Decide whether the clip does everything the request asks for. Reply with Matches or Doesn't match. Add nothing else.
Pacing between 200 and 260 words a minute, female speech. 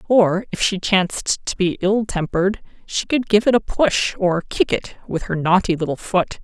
Matches